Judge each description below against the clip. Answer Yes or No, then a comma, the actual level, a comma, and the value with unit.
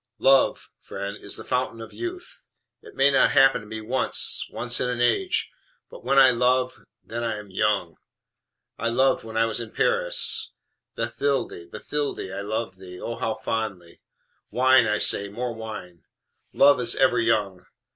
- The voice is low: Yes, low, 115 Hz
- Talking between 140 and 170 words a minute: Yes, average, 165 wpm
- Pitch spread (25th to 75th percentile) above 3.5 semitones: Yes, average, 4.0 semitones